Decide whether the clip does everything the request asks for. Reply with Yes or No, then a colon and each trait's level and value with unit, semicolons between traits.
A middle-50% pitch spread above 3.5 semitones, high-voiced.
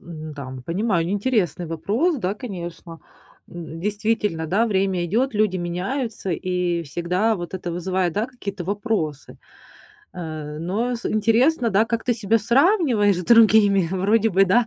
Yes: average, 4.6 semitones; high, 195 Hz